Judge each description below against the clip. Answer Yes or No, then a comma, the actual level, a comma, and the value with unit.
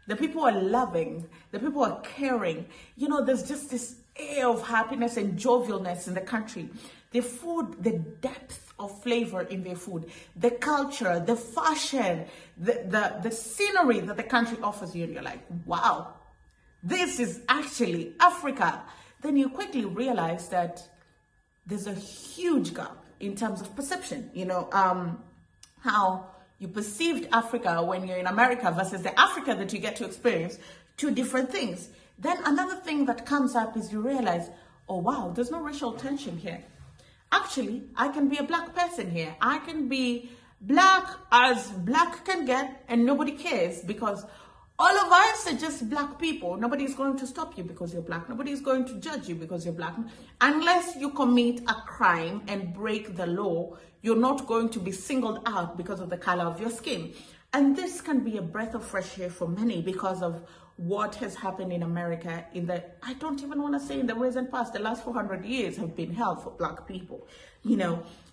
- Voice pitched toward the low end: No, high, 235 Hz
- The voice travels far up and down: Yes, wide, 6.4 semitones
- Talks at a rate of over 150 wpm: Yes, average, 185 wpm